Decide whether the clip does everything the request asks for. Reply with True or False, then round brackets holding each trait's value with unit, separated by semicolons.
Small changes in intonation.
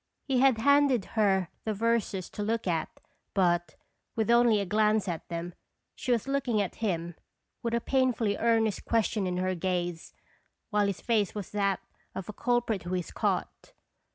False (3.9 semitones)